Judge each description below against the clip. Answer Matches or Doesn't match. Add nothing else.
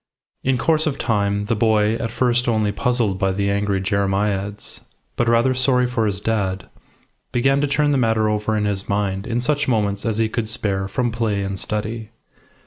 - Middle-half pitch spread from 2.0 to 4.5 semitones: Matches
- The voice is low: Matches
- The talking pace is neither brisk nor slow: Matches